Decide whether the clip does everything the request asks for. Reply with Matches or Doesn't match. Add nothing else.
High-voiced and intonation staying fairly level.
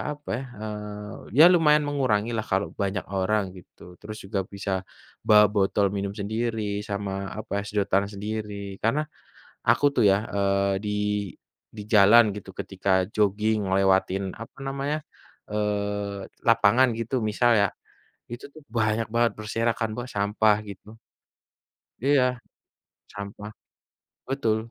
Doesn't match